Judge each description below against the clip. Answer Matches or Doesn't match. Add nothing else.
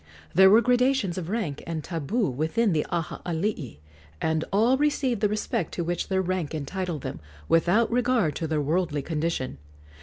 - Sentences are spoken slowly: Doesn't match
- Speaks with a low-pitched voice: Doesn't match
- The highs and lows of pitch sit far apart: Matches